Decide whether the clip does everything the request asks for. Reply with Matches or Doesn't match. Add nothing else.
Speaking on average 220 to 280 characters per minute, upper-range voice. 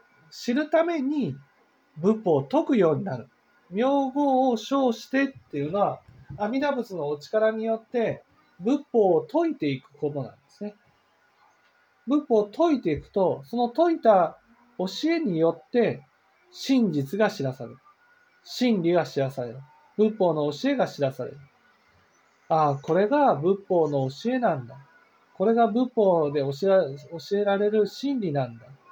Matches